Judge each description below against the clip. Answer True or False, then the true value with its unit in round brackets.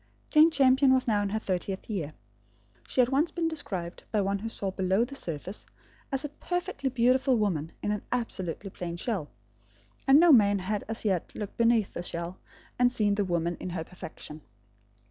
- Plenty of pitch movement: True (5.8 semitones)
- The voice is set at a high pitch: True (210 Hz)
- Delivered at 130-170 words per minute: False (185 wpm)